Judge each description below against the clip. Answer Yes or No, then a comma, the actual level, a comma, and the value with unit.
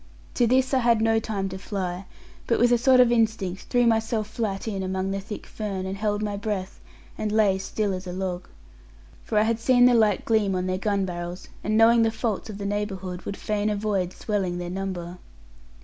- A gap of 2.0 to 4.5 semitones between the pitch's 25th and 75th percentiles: Yes, average, 2.8 semitones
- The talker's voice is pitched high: Yes, high, 205 Hz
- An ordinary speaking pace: No, fast, 210 wpm